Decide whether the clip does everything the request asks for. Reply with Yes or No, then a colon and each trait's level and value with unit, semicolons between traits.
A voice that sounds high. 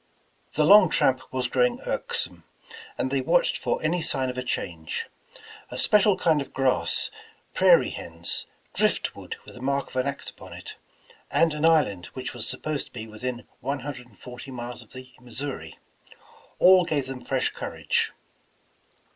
No: low, 130 Hz